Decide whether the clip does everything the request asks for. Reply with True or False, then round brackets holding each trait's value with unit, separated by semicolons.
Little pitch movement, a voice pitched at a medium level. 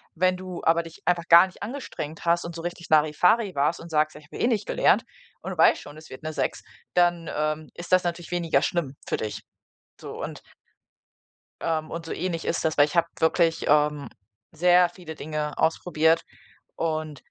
True (2.1 semitones; 165 Hz)